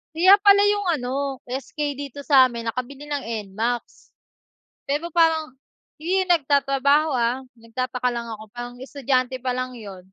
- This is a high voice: Yes, very high, 265 Hz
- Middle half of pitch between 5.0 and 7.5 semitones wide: No, average, 3.5 semitones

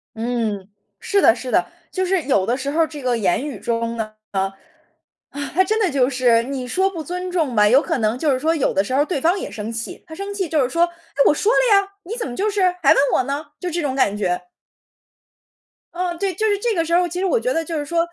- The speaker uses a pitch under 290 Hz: No, very high, 295 Hz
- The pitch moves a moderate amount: No, wide, 7.0 semitones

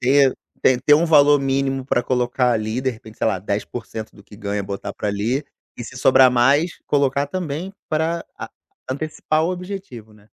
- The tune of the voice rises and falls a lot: No, average, 4.8 semitones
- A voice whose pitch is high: No, low, 130 Hz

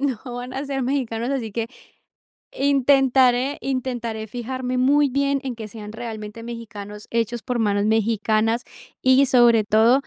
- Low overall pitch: No, high, 240 Hz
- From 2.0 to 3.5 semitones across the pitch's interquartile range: Yes, average, 3.0 semitones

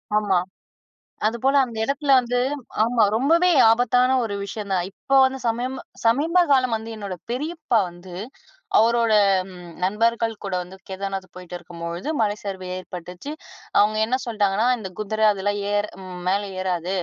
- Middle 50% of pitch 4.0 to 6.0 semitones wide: Yes, average, 4.5 semitones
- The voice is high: Yes, high, 215 Hz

